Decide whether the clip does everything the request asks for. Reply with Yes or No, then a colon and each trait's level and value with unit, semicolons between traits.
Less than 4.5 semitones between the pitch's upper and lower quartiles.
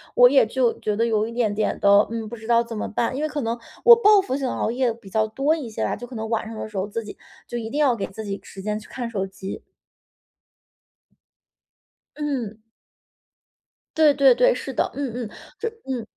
Yes: average, 3.6 semitones